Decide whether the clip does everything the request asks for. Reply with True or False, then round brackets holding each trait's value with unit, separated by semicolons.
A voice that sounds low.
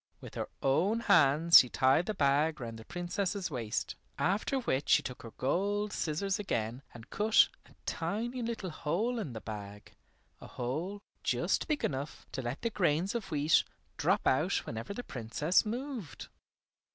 False (165 Hz)